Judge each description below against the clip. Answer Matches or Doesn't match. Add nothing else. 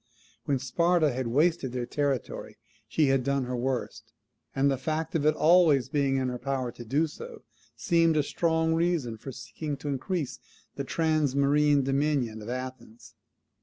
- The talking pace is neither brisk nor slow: Matches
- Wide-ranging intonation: Doesn't match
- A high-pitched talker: Doesn't match